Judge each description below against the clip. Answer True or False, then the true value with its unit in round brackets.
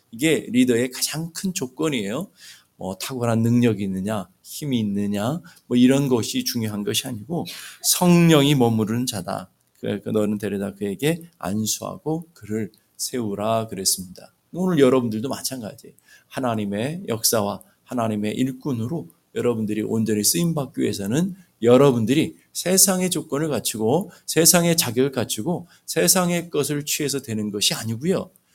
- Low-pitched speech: True (125 Hz)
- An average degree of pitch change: False (6.0 semitones)